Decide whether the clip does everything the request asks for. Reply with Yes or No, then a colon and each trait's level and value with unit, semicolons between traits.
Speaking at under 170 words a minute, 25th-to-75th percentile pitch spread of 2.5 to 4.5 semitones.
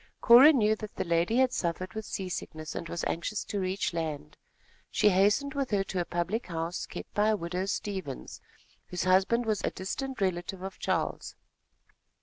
No: average, 175 wpm; average, 3.8 semitones